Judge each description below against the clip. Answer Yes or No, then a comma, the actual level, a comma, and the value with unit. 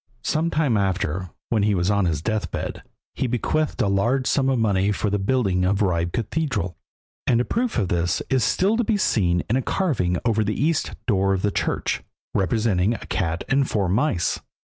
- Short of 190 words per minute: No, average, 195 wpm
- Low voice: Yes, low, 105 Hz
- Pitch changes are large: Yes, wide, 5.7 semitones